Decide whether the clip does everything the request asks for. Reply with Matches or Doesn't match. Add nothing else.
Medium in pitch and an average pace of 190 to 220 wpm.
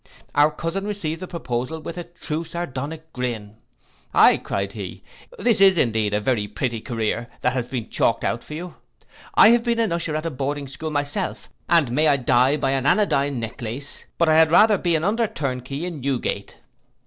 Matches